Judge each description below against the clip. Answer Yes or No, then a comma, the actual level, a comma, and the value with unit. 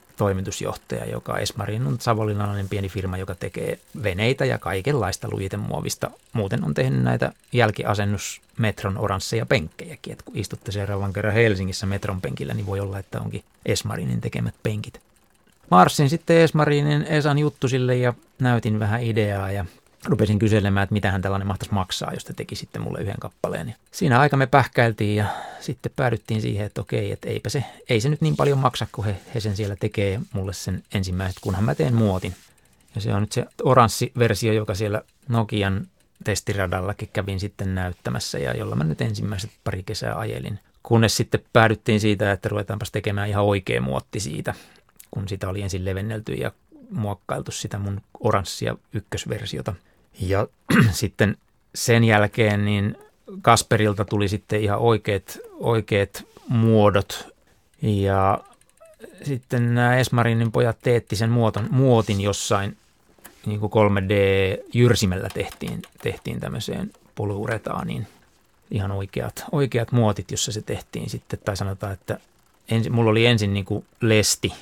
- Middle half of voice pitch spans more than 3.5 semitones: No, average, 2.8 semitones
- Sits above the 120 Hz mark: No, low, 105 Hz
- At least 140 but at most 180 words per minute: Yes, average, 150 wpm